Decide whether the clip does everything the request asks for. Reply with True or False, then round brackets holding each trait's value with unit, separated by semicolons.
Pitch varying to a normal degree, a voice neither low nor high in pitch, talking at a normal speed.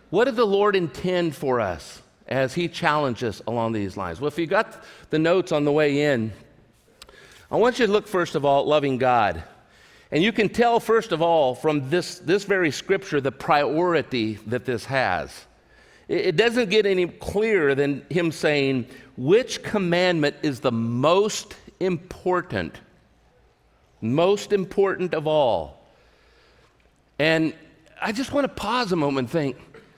False (6.5 semitones; 160 Hz; 160 wpm)